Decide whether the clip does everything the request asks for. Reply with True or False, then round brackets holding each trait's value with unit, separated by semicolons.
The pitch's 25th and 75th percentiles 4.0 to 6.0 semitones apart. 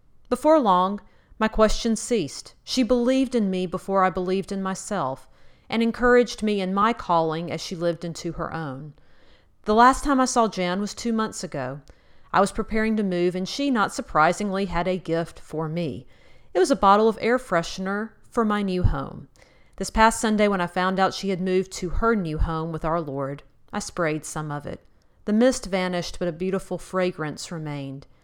True (4.7 semitones)